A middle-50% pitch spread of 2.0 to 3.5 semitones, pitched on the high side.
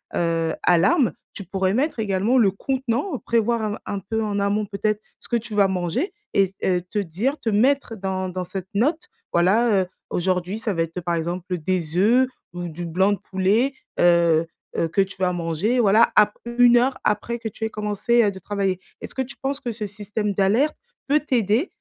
No: average, 4.2 semitones; high, 205 Hz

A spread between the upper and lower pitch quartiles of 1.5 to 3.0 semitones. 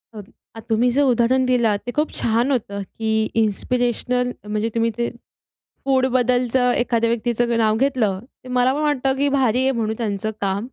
Yes: narrow, 2.5 semitones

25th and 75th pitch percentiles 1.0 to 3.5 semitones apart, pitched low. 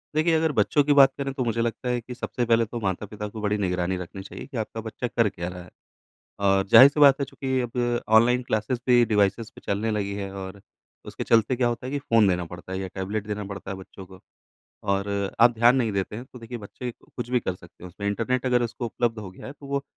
No: average, 4.0 semitones; low, 115 Hz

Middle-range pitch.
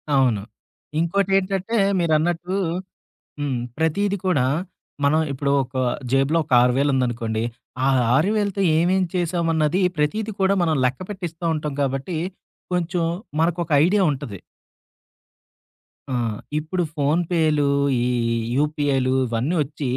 Yes: medium, 160 Hz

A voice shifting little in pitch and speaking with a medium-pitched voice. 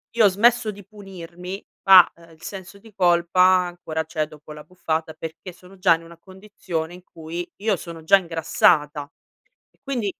No: average, 3.0 semitones; medium, 175 Hz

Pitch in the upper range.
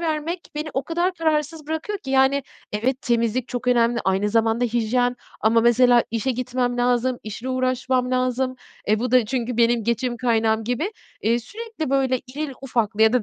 Yes: very high, 250 Hz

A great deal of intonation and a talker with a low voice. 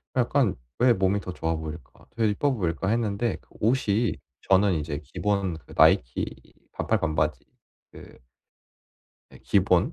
Yes: wide, 5.9 semitones; low, 100 Hz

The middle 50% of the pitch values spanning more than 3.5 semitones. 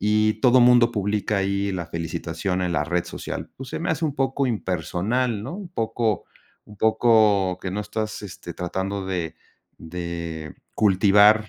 Yes: average, 4.0 semitones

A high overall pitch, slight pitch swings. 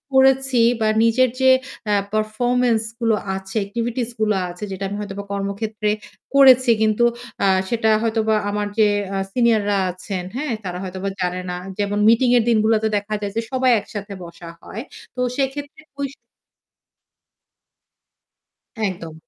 No: high, 220 Hz; average, 3.6 semitones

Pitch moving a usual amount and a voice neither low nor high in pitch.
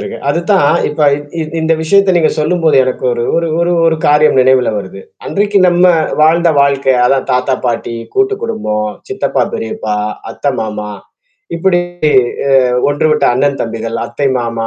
No: wide, 6.1 semitones; medium, 145 Hz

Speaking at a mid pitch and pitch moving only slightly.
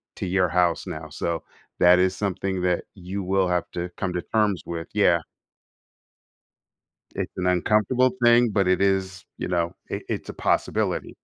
No: very low, 90 Hz; narrow, 1.8 semitones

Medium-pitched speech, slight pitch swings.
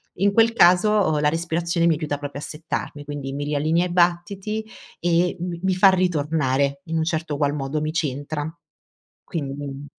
No: medium, 160 Hz; average, 3.3 semitones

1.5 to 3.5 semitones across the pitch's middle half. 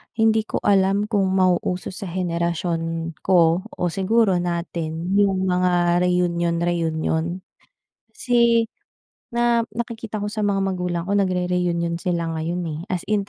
Yes: average, 2.9 semitones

